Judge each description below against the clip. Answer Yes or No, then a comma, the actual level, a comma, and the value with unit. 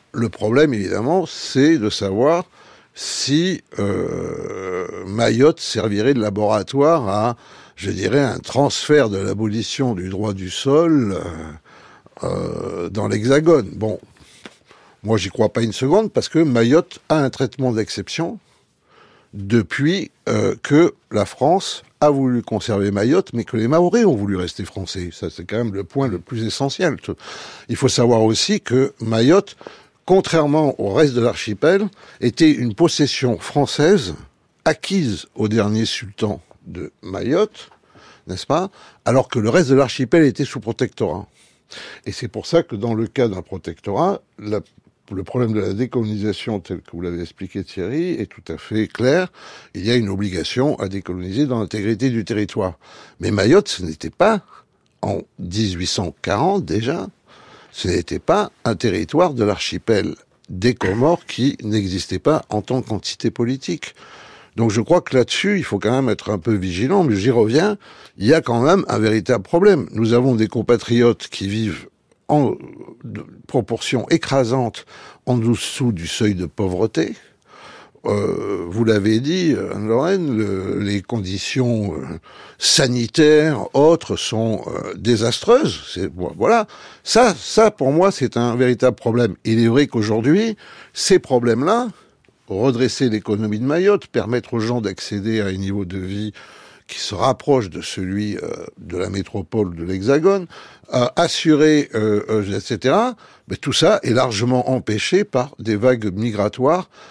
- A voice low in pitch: Yes, low, 115 Hz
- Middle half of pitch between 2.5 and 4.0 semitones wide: No, average, 4.8 semitones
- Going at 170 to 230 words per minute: No, average, 150 wpm